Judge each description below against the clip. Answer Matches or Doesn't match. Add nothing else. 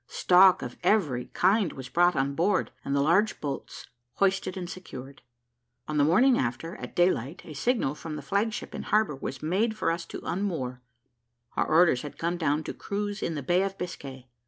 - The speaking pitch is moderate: Matches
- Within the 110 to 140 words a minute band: Doesn't match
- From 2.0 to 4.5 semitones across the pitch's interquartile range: Doesn't match